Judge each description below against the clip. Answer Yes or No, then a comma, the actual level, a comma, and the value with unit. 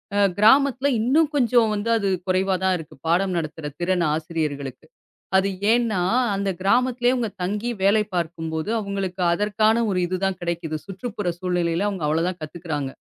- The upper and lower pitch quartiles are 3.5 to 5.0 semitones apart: Yes, average, 4.0 semitones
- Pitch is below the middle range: No, high, 190 Hz